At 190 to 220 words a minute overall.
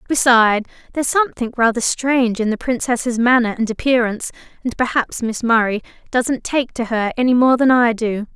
No: average, 170 wpm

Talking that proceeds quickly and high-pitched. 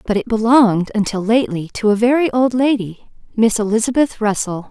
No: average, 165 wpm; high, 225 Hz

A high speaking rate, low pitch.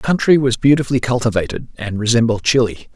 No: average, 165 wpm; low, 120 Hz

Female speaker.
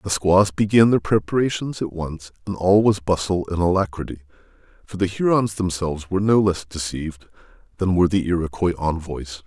No: male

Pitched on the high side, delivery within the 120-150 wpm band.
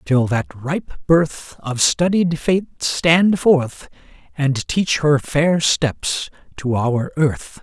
No: medium, 150 Hz; slow, 135 wpm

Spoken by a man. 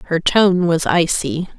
No: female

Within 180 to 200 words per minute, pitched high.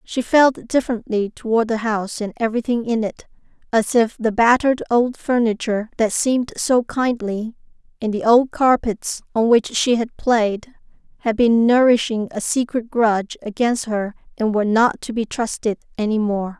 No: average, 165 wpm; high, 230 Hz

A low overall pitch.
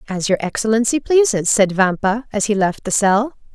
No: high, 215 Hz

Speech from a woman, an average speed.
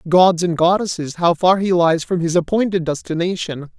No: male; average, 175 wpm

